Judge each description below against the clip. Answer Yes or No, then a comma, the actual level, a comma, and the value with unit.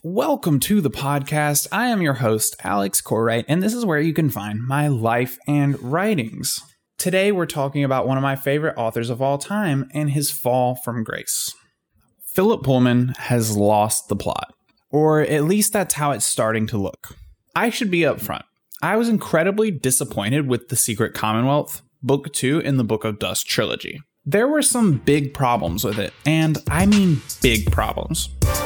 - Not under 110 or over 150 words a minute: No, average, 180 wpm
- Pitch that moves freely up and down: Yes, wide, 5.7 semitones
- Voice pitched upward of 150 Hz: No, medium, 140 Hz